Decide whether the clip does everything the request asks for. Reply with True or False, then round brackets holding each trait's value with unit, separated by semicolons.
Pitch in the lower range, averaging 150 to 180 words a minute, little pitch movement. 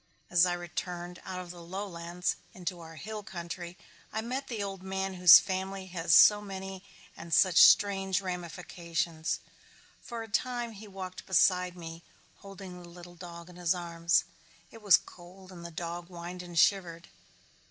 False (180 Hz; 165 wpm; 2.0 semitones)